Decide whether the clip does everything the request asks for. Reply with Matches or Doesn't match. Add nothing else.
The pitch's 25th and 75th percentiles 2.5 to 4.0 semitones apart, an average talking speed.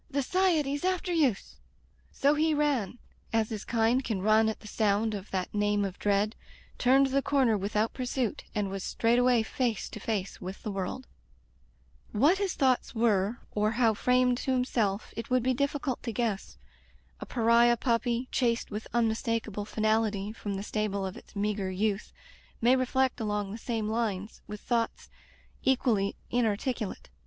Matches